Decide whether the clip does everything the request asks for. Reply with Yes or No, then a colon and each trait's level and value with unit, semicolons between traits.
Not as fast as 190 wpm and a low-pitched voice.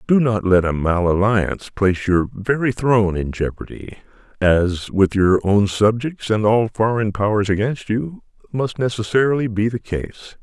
Yes: average, 160 wpm; low, 105 Hz